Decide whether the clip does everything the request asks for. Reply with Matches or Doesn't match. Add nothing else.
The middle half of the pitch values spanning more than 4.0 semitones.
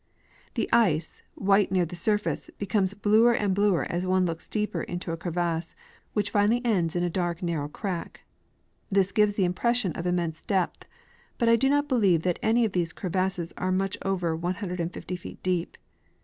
Doesn't match